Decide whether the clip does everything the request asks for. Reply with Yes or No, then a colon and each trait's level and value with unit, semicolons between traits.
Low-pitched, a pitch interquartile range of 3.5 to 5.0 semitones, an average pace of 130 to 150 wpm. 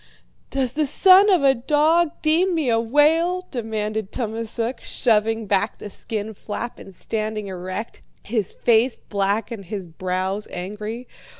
No: high, 225 Hz; average, 4.7 semitones; average, 140 wpm